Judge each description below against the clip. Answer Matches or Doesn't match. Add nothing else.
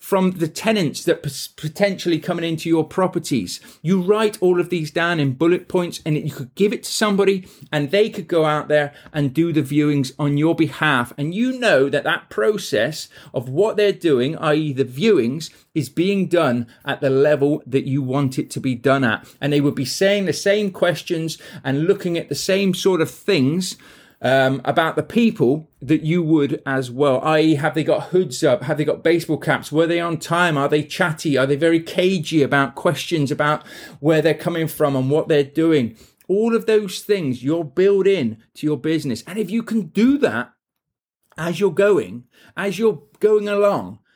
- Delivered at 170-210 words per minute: Matches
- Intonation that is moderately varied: Matches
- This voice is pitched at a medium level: Matches